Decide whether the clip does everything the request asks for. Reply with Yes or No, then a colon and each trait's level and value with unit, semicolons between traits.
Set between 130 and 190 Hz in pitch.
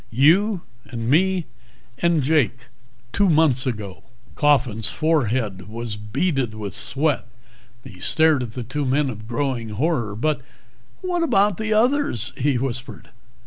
Yes: low, 135 Hz